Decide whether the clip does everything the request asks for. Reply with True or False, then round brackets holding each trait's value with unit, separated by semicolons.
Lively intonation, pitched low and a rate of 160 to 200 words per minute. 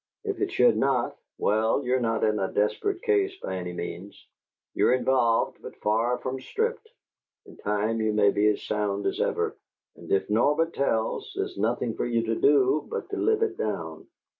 True (5.7 semitones; 115 Hz; 185 wpm)